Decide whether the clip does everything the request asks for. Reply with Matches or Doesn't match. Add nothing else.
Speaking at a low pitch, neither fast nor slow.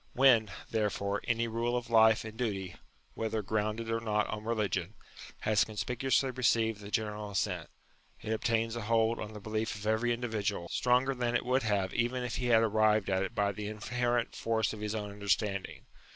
Matches